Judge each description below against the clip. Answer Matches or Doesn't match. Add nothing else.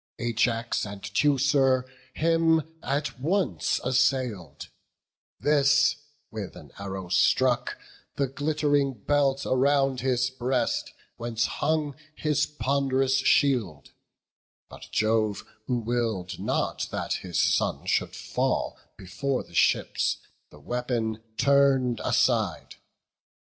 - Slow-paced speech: Matches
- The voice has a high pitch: Doesn't match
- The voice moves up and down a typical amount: Matches